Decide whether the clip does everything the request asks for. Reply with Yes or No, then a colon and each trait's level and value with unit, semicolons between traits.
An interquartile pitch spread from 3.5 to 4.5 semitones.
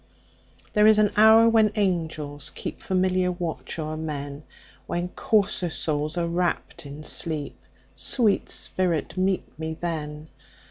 Yes: average, 3.8 semitones